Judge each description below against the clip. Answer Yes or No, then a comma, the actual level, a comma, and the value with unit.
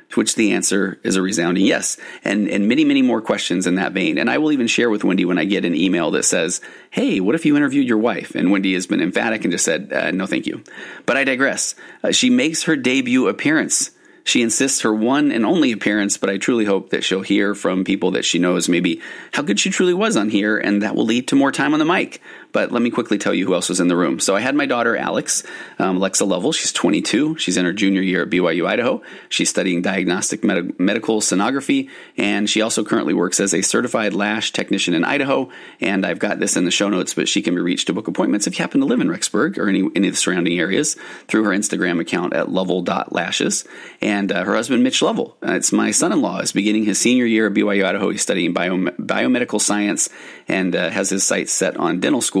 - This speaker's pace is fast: Yes, fast, 245 wpm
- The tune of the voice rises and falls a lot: Yes, wide, 8.5 semitones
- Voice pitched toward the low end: Yes, low, 105 Hz